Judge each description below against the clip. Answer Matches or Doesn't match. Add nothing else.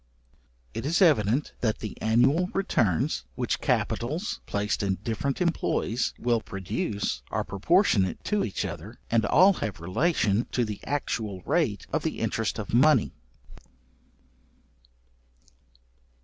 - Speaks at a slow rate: Matches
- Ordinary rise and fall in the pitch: Doesn't match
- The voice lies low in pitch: Matches